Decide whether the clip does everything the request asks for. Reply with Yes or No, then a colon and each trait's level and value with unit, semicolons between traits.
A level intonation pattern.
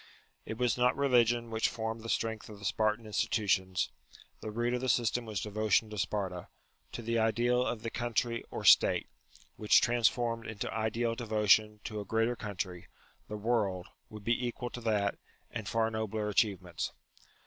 Yes: narrow, 1.9 semitones